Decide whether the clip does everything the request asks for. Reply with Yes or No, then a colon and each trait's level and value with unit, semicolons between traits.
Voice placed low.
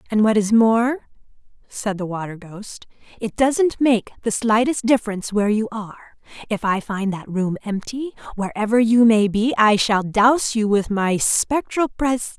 No: high, 220 Hz